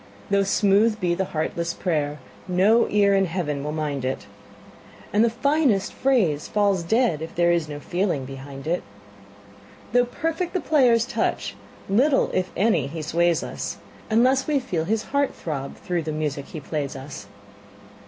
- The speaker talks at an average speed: Yes, average, 165 wpm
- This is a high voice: No, medium, 180 Hz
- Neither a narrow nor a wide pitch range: No, wide, 6.8 semitones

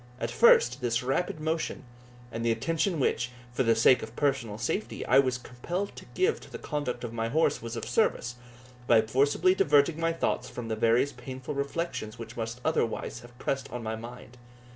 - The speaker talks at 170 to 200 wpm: Yes, average, 190 wpm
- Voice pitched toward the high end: No, low, 125 Hz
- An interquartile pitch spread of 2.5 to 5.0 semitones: Yes, average, 4.3 semitones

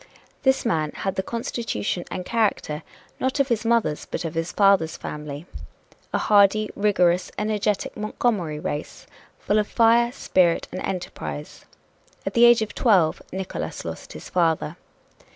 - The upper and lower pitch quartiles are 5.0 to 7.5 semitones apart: Yes, average, 5.3 semitones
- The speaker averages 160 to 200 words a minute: No, average, 145 wpm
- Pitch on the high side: Yes, high, 195 Hz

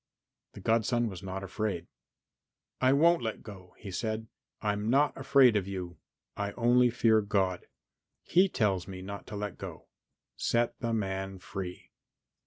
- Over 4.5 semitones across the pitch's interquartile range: No, average, 3.6 semitones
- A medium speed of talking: Yes, average, 150 wpm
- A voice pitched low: Yes, low, 105 Hz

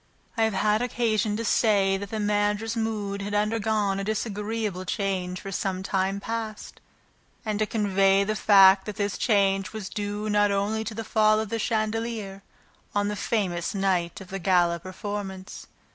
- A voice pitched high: Yes, high, 205 Hz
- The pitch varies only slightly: Yes, narrow, 1.9 semitones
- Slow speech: No, average, 170 wpm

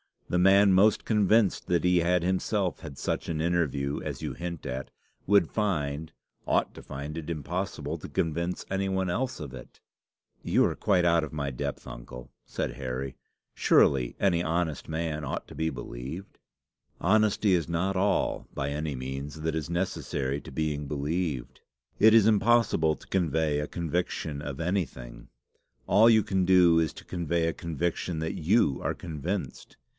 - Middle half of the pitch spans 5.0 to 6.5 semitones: No, average, 4.2 semitones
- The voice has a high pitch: No, very low, 85 Hz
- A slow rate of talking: No, average, 165 wpm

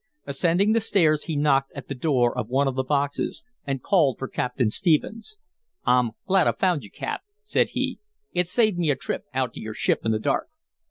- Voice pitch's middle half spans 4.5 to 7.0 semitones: Yes, wide, 5.6 semitones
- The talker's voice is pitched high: No, medium, 140 Hz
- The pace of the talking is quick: Yes, fast, 210 wpm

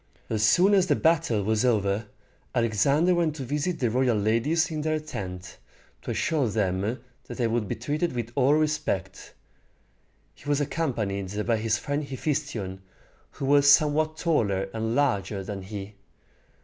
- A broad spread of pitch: Yes, wide, 6.3 semitones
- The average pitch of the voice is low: Yes, low, 120 Hz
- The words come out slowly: No, average, 155 wpm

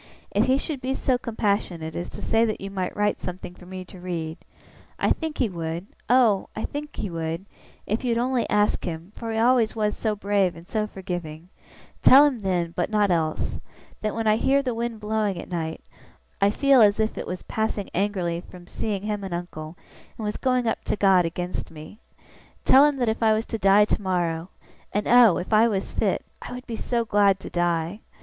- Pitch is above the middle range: Yes, high, 205 Hz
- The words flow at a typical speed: No, fast, 215 wpm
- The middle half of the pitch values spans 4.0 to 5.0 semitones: Yes, average, 4.3 semitones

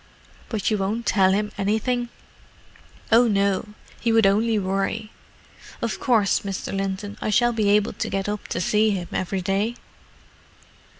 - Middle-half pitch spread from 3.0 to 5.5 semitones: No, narrow, 2.4 semitones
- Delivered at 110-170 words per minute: Yes, average, 155 wpm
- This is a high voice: Yes, high, 210 Hz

